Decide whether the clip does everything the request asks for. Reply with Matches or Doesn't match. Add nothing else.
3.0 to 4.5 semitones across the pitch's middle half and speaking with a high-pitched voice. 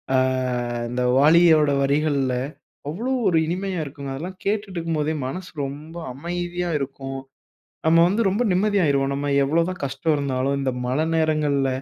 Doesn't match